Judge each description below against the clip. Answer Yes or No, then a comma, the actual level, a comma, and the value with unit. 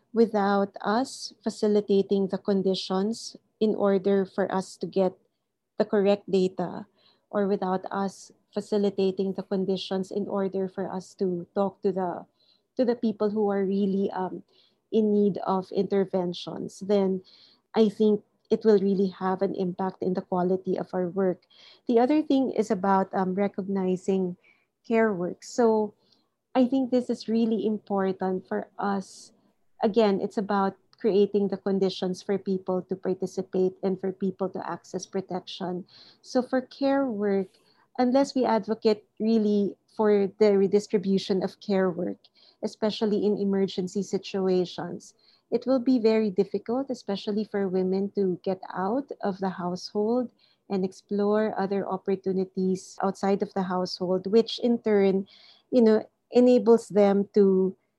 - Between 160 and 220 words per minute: No, average, 140 wpm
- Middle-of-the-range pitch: No, high, 200 Hz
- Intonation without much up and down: Yes, narrow, 2.2 semitones